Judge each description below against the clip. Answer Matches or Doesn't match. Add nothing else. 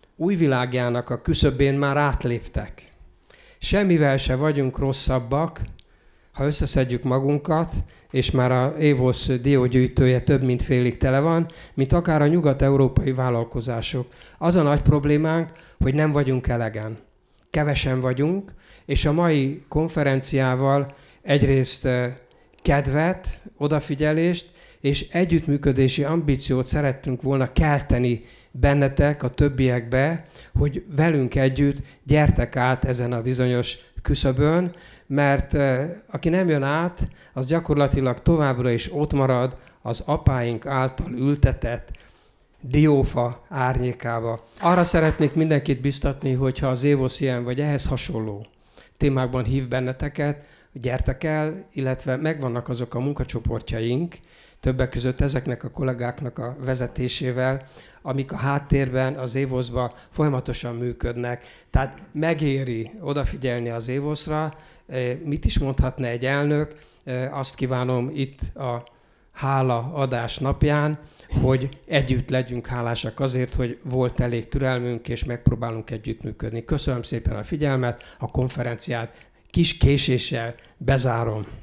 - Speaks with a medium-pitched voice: Doesn't match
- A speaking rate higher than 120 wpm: Doesn't match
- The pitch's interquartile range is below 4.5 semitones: Matches